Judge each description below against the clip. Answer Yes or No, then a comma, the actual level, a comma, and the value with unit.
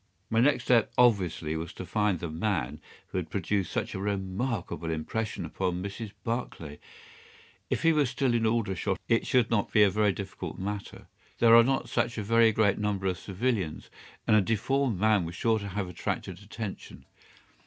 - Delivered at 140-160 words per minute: No, average, 180 wpm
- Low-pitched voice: Yes, low, 105 Hz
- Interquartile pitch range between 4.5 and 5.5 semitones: No, average, 3.6 semitones